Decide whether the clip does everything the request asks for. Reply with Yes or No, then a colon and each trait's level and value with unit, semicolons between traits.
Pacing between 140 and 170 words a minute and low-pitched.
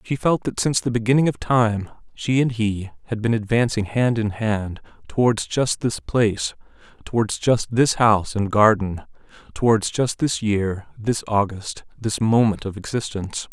Yes: average, 165 wpm; low, 110 Hz